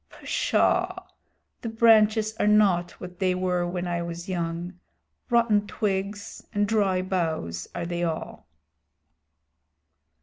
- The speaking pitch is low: No, medium, 185 Hz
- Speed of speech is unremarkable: No, slow, 115 wpm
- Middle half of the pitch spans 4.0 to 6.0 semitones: No, average, 3.4 semitones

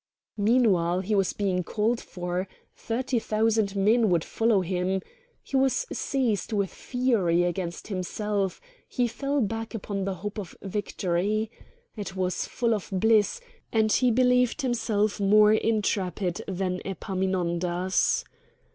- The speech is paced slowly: Yes, slow, 130 wpm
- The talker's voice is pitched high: Yes, high, 205 Hz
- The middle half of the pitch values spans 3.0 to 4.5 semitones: Yes, average, 3.4 semitones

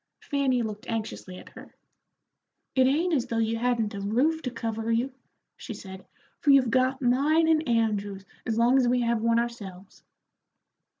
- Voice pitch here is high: Yes, high, 235 Hz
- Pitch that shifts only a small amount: No, average, 3.0 semitones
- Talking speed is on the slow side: No, average, 170 wpm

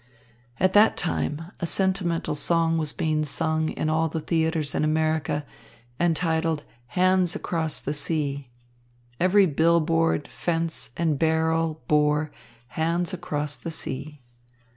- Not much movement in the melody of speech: Yes, narrow, 1.7 semitones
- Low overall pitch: No, medium, 160 Hz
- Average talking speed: No, slow, 125 wpm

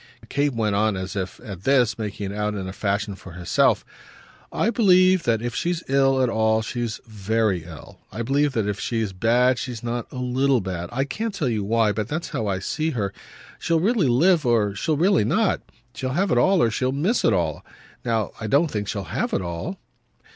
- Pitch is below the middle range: Yes, low, 115 Hz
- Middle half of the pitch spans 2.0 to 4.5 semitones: No, wide, 5.4 semitones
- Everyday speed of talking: No, fast, 210 wpm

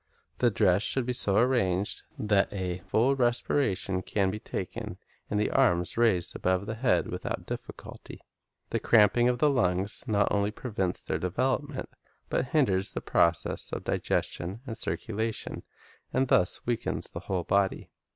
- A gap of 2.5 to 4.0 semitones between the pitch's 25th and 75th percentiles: No, average, 4.5 semitones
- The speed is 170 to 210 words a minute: No, average, 155 wpm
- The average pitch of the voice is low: Yes, low, 105 Hz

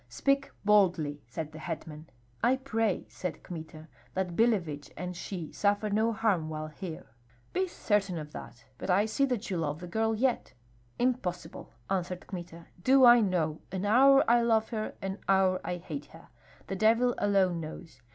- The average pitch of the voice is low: No, high, 190 Hz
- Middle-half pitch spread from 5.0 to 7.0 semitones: Yes, wide, 5.4 semitones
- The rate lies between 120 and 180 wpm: Yes, average, 170 wpm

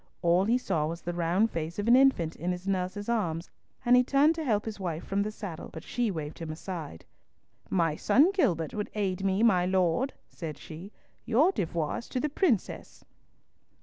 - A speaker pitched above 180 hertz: Yes, high, 190 Hz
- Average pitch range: No, wide, 5.7 semitones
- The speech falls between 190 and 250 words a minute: Yes, average, 195 wpm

